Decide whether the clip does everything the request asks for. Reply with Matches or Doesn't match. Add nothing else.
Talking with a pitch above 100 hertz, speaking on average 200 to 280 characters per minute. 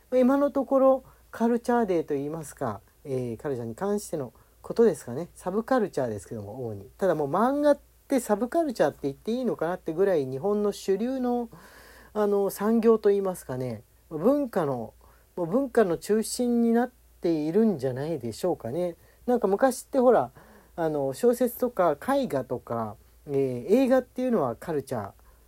Doesn't match